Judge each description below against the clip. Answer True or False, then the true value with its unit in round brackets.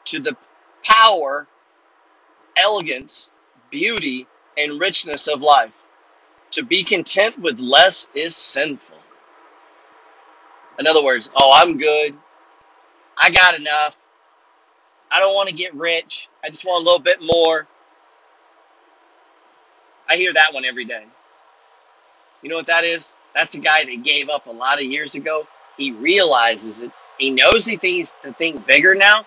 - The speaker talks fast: False (145 wpm)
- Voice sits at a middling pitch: True (160 Hz)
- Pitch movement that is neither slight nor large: True (3.7 semitones)